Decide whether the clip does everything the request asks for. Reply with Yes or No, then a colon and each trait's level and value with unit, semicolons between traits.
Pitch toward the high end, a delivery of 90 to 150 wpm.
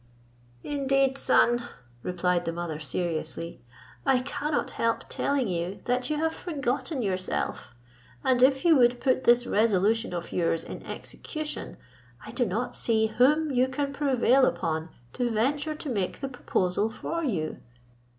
Yes: high, 245 Hz; average, 145 wpm